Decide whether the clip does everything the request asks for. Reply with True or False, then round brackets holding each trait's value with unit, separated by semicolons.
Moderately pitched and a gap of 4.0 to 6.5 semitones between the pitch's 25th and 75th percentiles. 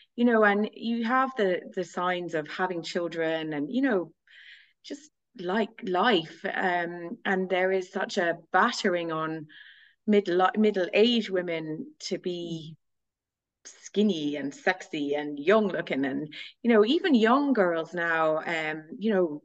True (180 Hz; 4.7 semitones)